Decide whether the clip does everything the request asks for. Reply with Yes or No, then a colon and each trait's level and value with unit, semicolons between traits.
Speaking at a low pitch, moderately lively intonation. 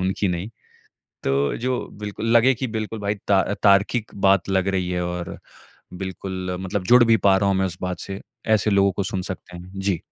No: very low, 95 Hz; narrow, 2.1 semitones